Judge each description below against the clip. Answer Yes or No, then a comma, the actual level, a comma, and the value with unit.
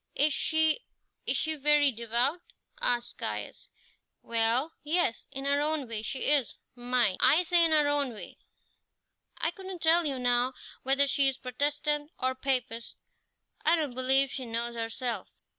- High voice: Yes, very high, 270 Hz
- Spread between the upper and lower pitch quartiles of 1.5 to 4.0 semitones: Yes, average, 3.7 semitones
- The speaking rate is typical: Yes, average, 155 wpm